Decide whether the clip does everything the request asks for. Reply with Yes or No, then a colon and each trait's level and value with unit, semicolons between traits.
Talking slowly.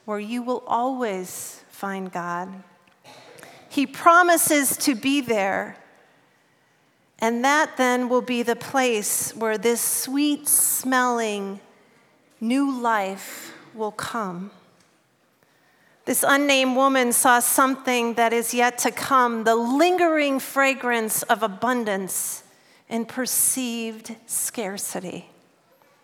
Yes: slow, 100 wpm